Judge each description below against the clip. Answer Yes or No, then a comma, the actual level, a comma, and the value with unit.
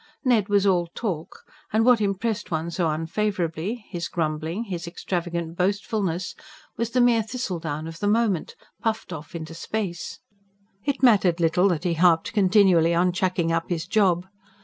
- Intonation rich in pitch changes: No, average, 4.1 semitones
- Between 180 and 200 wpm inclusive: No, average, 155 wpm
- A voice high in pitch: No, medium, 180 Hz